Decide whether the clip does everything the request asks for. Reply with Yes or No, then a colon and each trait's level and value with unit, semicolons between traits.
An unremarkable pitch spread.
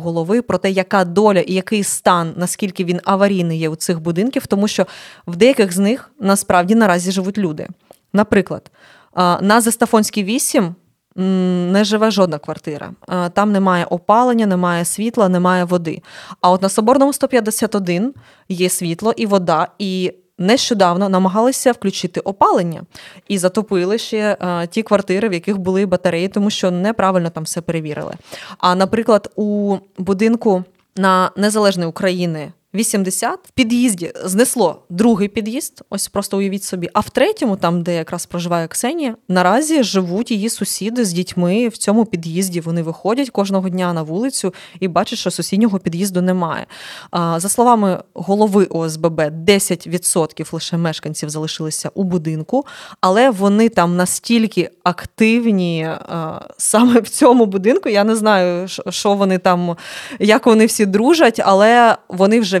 Yes: average, 3.5 semitones